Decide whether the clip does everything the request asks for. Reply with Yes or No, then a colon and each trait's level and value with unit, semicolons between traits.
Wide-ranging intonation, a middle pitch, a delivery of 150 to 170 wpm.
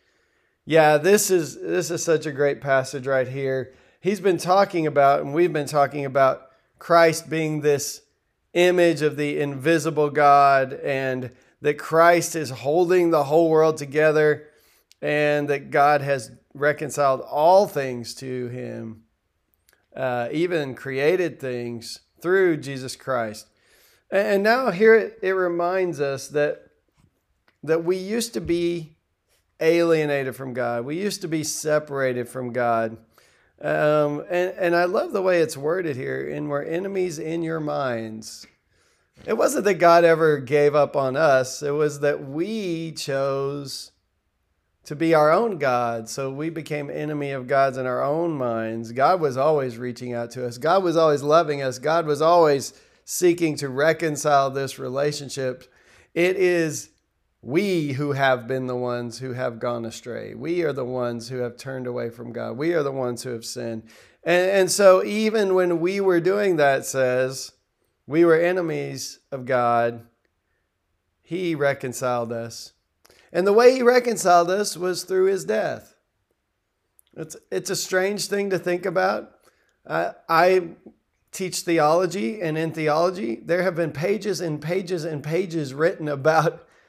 No: average, 4.8 semitones; medium, 150 Hz; average, 155 wpm